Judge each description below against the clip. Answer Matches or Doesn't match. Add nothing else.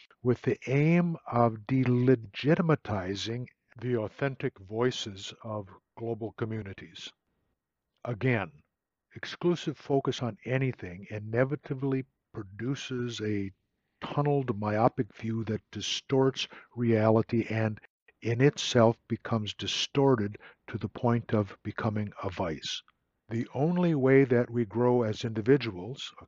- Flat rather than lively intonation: Doesn't match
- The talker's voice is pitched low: Matches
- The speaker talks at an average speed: Doesn't match